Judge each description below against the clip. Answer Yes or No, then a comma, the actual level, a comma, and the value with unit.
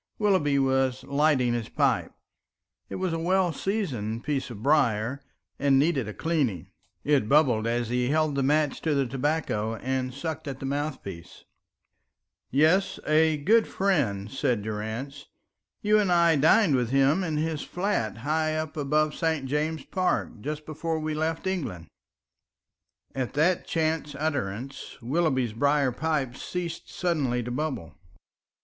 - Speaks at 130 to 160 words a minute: Yes, average, 145 wpm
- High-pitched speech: No, medium, 145 Hz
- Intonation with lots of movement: No, average, 4.2 semitones